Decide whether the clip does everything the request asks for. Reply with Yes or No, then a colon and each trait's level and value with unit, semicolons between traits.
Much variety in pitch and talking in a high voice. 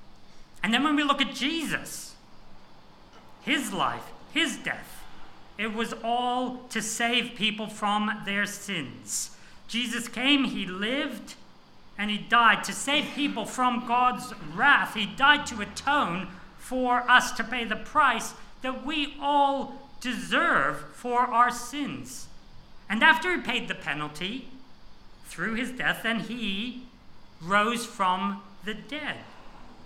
No: average, 3.9 semitones; high, 240 Hz